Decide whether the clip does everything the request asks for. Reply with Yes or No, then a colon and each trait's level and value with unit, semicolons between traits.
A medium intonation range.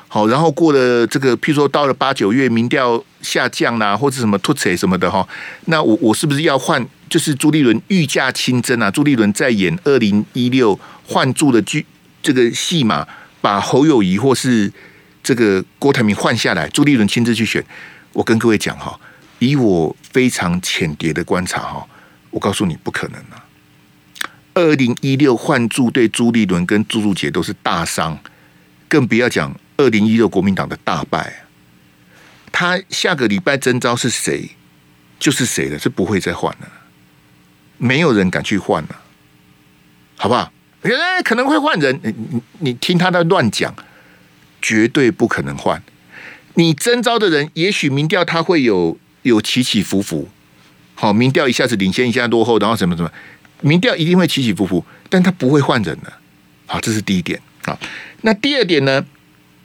No: wide, 7.2 semitones